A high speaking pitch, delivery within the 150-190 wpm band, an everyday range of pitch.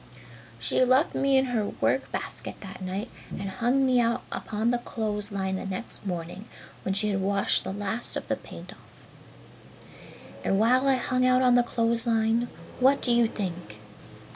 Yes: high, 225 Hz; average, 180 wpm; average, 4.1 semitones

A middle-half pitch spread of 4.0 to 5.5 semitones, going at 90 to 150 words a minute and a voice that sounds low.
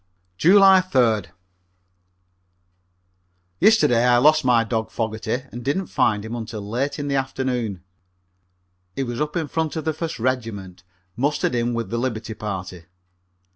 Yes: average, 4.5 semitones; average, 140 wpm; low, 120 Hz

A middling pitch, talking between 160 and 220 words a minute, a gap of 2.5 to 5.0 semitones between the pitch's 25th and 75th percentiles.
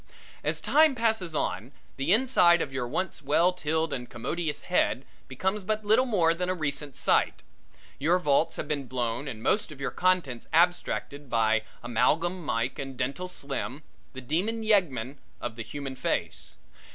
No: medium, 150 Hz; average, 165 wpm; wide, 5.6 semitones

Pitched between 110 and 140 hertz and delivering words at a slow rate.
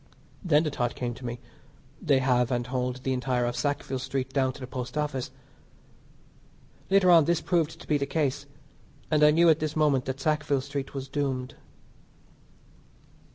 No: low, 135 Hz; average, 175 wpm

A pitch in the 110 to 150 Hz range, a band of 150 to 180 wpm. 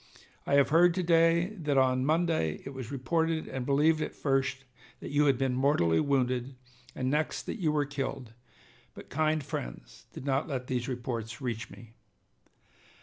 Yes: low, 135 Hz; average, 170 wpm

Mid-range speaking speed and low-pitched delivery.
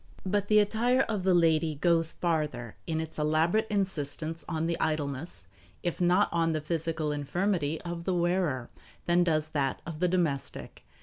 No: average, 165 wpm; medium, 165 Hz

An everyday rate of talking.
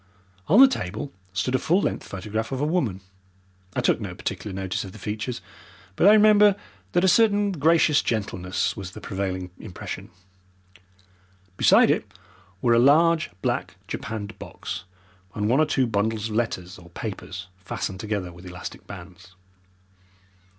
Yes: average, 155 wpm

